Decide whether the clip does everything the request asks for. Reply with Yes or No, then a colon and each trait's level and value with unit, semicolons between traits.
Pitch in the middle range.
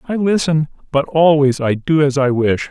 Yes: medium, 145 Hz